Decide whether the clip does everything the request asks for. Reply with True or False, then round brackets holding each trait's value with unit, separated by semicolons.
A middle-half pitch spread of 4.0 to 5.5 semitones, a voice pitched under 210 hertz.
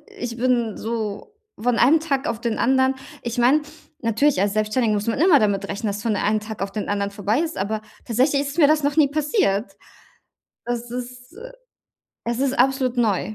False (4.5 semitones; 240 Hz)